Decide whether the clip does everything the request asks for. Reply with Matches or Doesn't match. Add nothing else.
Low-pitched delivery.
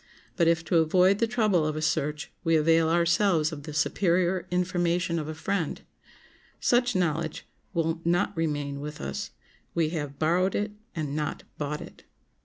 Doesn't match